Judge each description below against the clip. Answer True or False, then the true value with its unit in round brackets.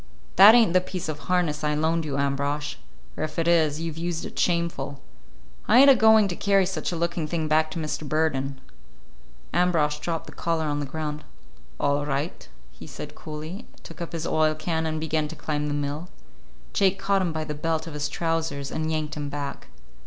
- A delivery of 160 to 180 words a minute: False (205 wpm)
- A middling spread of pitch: False (2.3 semitones)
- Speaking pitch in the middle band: True (155 Hz)